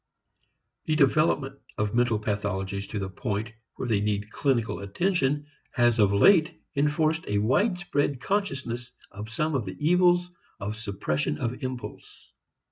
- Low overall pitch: Yes, low, 120 Hz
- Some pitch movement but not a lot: No, wide, 6.6 semitones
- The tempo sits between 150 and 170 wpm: No, slow, 135 wpm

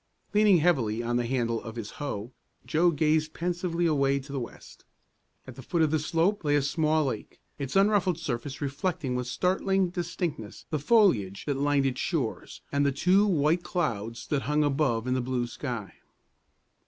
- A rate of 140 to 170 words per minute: No, average, 180 wpm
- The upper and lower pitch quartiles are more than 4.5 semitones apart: Yes, average, 5.3 semitones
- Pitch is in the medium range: Yes, medium, 145 Hz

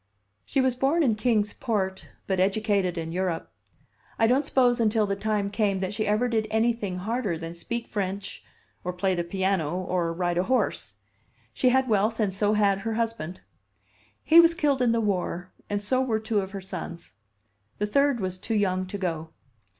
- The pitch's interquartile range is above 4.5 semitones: No, average, 3.7 semitones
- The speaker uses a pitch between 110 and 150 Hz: No, high, 205 Hz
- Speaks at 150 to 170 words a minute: No, average, 190 wpm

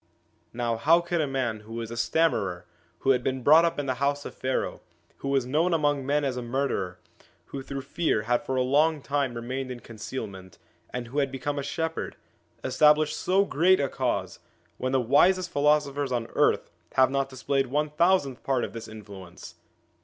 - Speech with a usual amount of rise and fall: Yes, average, 3.5 semitones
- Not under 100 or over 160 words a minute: No, average, 195 wpm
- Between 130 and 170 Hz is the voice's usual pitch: Yes, low, 135 Hz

